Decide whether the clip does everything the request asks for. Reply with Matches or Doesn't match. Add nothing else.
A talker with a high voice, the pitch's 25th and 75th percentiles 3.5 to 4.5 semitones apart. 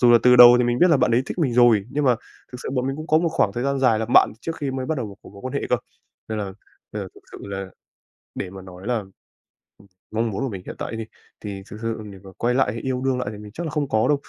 Doesn't match